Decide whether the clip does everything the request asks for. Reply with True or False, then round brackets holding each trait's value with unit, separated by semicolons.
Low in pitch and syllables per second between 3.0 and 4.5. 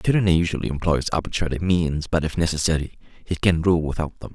False (80 Hz; 6.2 syllables/s)